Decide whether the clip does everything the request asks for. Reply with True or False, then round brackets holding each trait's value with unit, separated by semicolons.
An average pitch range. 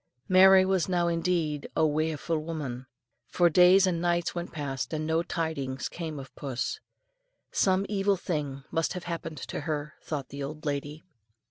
True (3.1 semitones)